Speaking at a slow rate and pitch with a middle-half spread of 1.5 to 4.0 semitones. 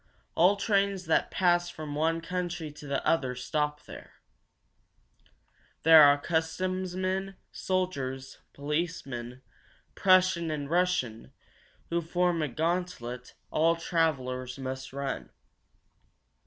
No: slow, 105 wpm; average, 4.6 semitones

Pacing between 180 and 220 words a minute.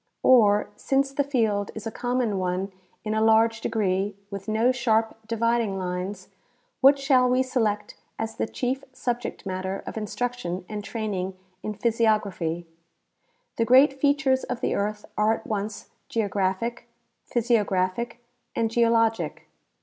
No: average, 140 wpm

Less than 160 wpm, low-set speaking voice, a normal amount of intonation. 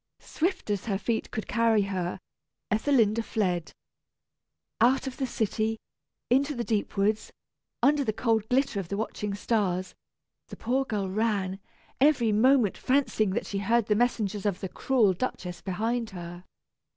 No: average, 150 wpm; high, 220 Hz; average, 3.6 semitones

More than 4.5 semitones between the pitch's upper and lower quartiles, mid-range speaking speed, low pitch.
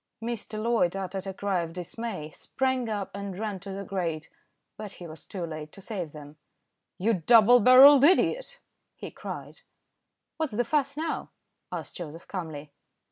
No: wide, 5.5 semitones; average, 160 wpm; high, 200 Hz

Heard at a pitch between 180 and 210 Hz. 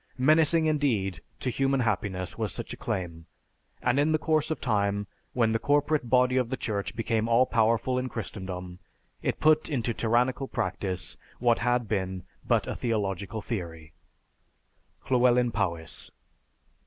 No: low, 115 Hz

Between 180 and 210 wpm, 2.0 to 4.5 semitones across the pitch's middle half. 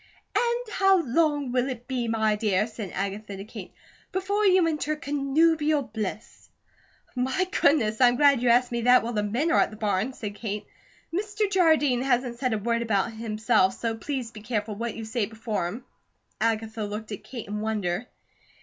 No: average, 185 wpm; average, 4.9 semitones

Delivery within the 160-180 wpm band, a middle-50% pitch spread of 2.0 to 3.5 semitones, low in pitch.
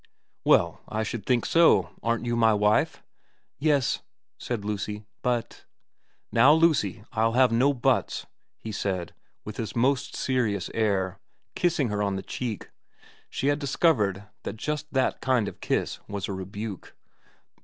No: average, 165 wpm; average, 4.2 semitones; low, 115 Hz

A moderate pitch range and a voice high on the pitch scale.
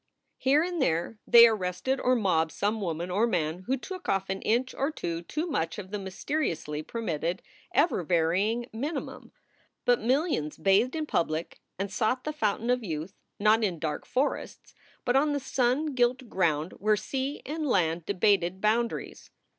No: wide, 6.6 semitones; high, 215 Hz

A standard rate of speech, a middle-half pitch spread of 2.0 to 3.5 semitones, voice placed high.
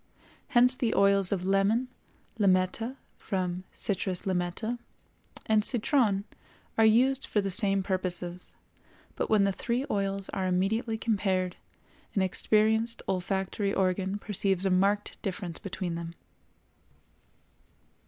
No: slow, 115 wpm; average, 2.9 semitones; high, 195 Hz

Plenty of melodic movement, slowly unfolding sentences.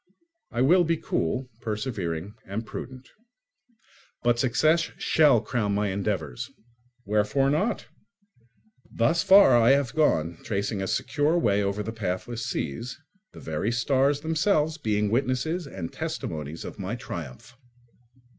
Yes: wide, 6.0 semitones; slow, 125 wpm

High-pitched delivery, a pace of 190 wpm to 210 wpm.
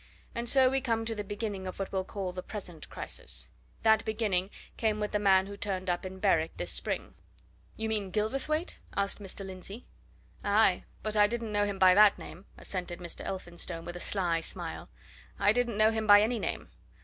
Yes: high, 205 Hz; average, 195 wpm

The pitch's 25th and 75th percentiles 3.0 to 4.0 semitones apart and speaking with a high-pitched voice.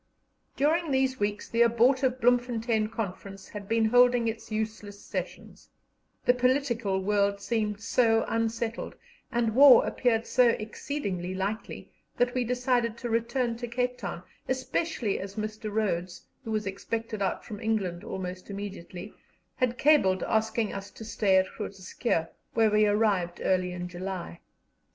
Yes: average, 3.4 semitones; high, 220 Hz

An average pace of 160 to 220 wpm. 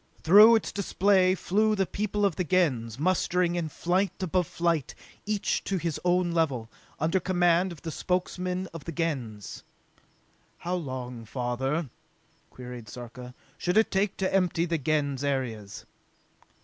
No: average, 145 wpm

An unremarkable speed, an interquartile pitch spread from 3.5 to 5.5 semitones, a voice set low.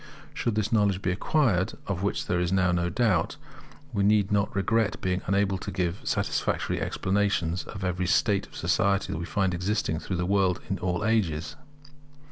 No: average, 185 wpm; narrow, 2.5 semitones; very low, 95 Hz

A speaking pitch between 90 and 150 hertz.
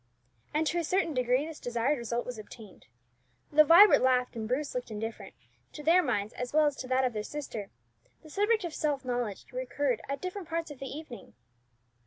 No: very high, 265 Hz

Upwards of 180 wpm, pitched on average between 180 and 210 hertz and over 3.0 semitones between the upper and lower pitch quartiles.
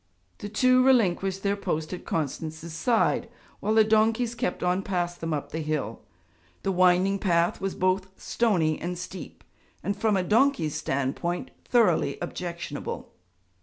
No: average, 145 wpm; medium, 185 Hz; average, 4.0 semitones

